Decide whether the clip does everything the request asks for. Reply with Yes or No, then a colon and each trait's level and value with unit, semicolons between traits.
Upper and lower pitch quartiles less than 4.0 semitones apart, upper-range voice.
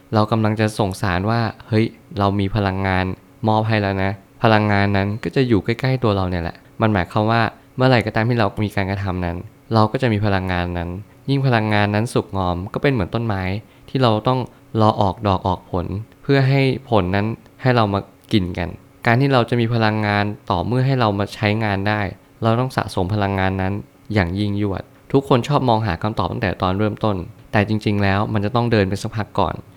No: average, 3.0 semitones; low, 105 Hz